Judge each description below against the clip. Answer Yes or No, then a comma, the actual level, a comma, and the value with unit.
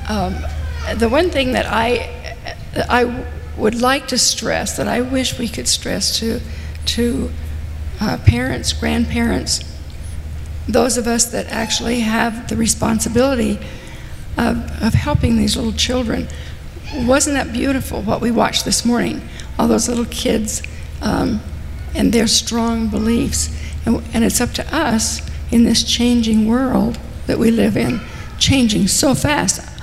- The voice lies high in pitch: Yes, high, 225 Hz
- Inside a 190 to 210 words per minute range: No, average, 145 wpm